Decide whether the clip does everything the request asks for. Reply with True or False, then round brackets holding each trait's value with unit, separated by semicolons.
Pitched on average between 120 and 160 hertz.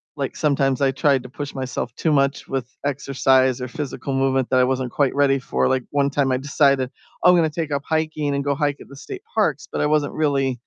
True (140 Hz)